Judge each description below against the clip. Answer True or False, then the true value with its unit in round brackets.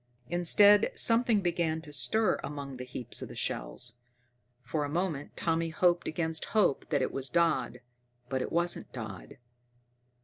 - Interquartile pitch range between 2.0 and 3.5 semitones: False (4.7 semitones)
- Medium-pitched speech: True (160 Hz)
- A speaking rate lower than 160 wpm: True (145 wpm)